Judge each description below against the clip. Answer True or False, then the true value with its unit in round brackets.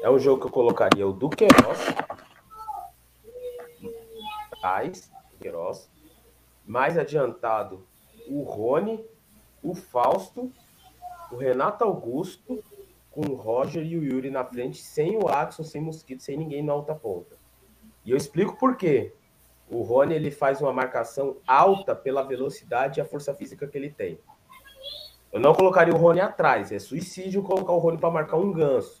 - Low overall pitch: False (190 Hz)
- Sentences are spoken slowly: False (150 wpm)